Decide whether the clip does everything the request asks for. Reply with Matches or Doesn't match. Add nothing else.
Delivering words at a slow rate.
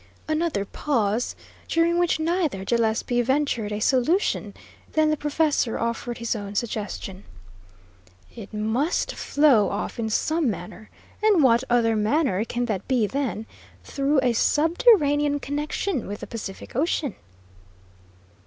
Matches